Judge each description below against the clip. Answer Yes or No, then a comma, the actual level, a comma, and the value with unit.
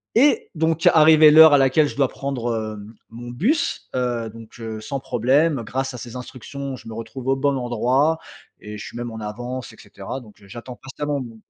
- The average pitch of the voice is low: Yes, low, 125 Hz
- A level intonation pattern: No, average, 3.7 semitones